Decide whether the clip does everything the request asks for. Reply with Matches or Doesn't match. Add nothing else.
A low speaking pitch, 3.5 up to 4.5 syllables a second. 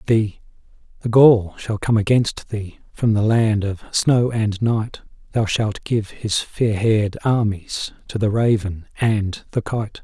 Matches